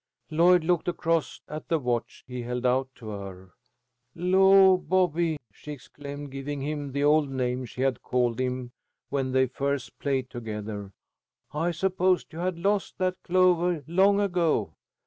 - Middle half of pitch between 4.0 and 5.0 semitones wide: No, wide, 5.6 semitones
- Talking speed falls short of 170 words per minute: Yes, average, 150 wpm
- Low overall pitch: No, medium, 145 Hz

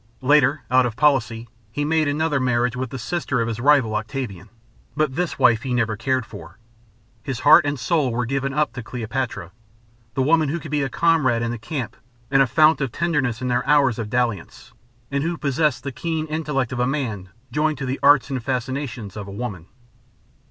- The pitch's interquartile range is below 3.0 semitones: No, average, 4.0 semitones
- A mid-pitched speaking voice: No, low, 130 Hz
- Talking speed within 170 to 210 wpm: Yes, average, 200 wpm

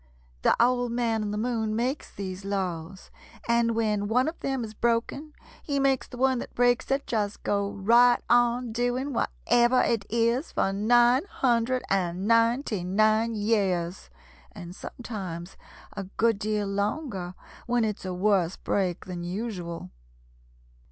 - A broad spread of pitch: No, average, 3.7 semitones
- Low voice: No, high, 220 Hz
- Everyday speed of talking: Yes, average, 145 wpm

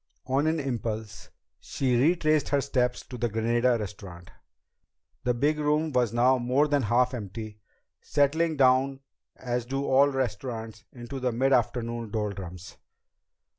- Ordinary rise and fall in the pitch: Yes, average, 3.4 semitones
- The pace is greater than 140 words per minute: No, slow, 135 wpm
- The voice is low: Yes, low, 125 Hz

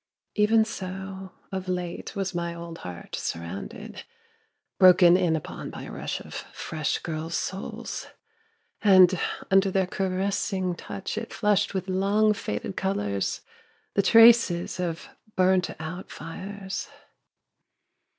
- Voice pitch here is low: No, medium, 185 Hz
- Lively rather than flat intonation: No, narrow, 2.4 semitones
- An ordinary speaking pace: No, slow, 120 wpm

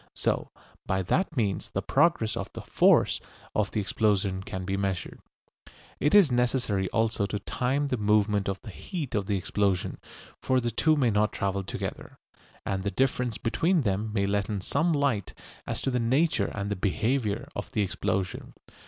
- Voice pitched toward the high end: No, low, 105 Hz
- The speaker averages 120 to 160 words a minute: No, average, 175 wpm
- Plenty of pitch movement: No, average, 4.6 semitones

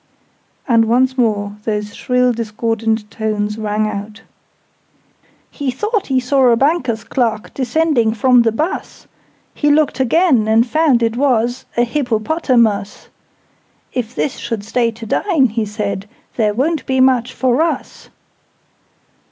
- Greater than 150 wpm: No, slow, 135 wpm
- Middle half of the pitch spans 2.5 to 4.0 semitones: Yes, average, 3.3 semitones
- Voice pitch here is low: No, high, 235 Hz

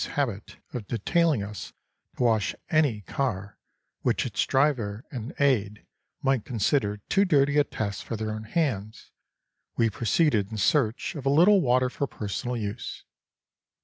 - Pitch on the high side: No, low, 120 Hz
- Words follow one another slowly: No, average, 150 wpm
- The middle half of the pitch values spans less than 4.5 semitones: No, average, 5.1 semitones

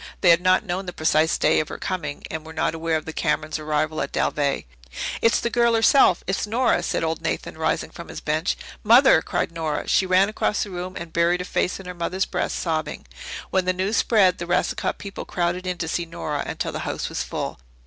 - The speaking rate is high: Yes, fast, 225 wpm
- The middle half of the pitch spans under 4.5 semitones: Yes, average, 2.9 semitones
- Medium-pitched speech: Yes, medium, 175 Hz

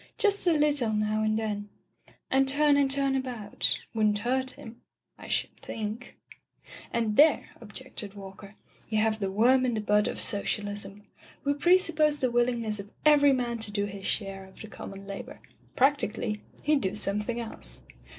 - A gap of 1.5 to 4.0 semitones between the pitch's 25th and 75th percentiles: No, average, 4.5 semitones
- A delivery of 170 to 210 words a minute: Yes, average, 175 wpm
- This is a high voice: Yes, high, 225 Hz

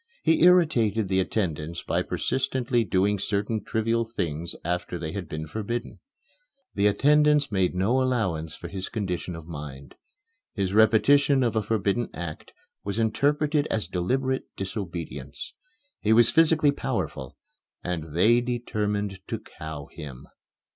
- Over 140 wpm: No, slow, 135 wpm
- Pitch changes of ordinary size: No, wide, 5.7 semitones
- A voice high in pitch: No, low, 105 Hz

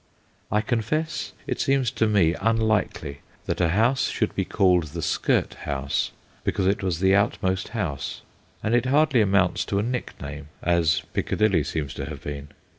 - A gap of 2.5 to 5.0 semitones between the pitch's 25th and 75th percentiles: No, wide, 5.6 semitones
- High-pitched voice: No, very low, 95 Hz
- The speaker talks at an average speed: Yes, average, 165 wpm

